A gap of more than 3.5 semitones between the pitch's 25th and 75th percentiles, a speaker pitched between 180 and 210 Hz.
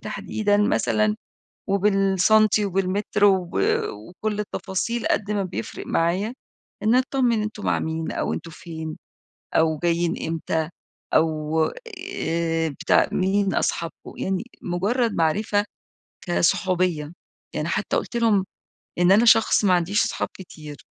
Yes: average, 4.1 semitones; high, 190 Hz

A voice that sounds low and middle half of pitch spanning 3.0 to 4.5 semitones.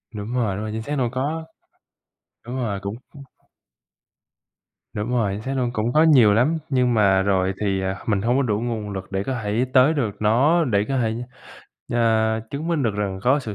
Yes: low, 110 Hz; average, 4.0 semitones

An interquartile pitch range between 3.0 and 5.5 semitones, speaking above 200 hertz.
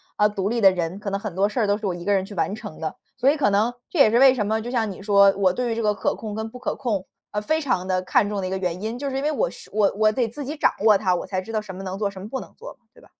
Yes: average, 3.6 semitones; high, 210 Hz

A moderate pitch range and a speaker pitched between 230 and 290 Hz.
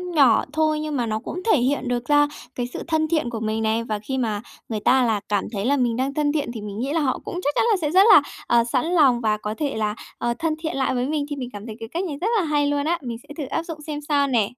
Yes: average, 4.8 semitones; very high, 265 Hz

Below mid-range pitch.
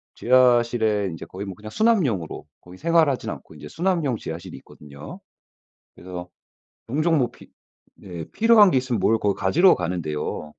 Yes: low, 115 Hz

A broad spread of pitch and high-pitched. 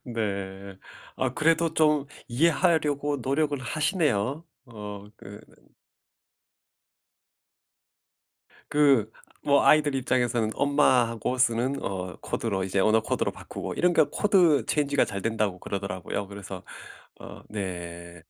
No: wide, 6.5 semitones; low, 120 Hz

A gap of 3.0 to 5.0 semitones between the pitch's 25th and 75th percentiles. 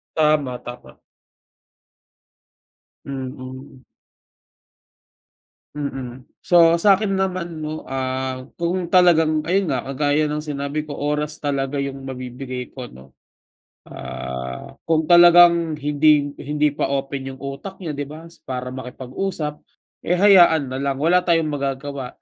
Yes: average, 3.8 semitones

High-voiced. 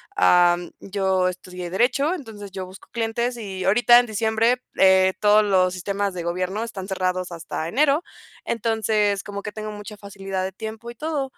Yes: high, 205 Hz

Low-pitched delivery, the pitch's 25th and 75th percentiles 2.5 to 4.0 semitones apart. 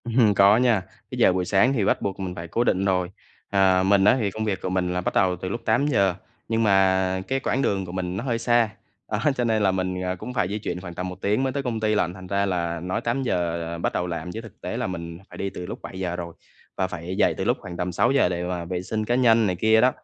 Yes: very low, 95 Hz; average, 3.5 semitones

